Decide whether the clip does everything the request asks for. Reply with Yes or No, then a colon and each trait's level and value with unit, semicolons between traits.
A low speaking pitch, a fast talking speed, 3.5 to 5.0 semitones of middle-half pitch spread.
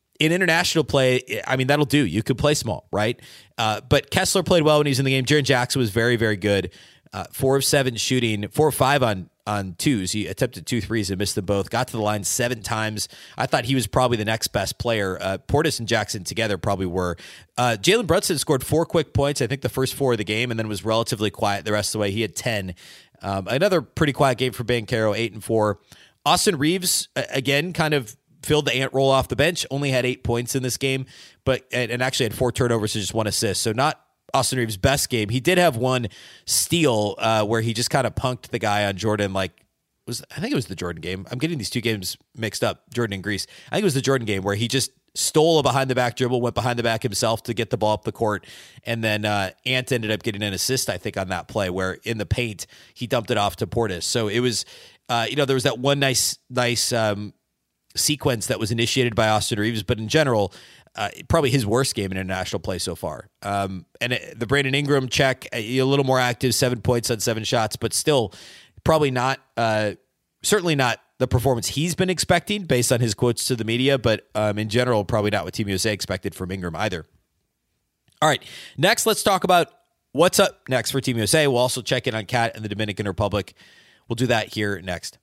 Yes: low, 120 Hz; fast, 240 wpm; average, 4.1 semitones